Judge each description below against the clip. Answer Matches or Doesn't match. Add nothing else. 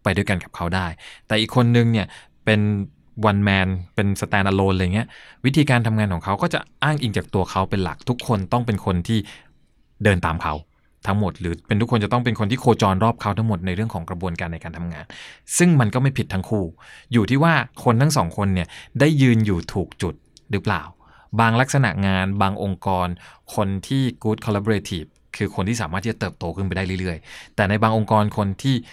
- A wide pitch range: Doesn't match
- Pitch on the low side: Matches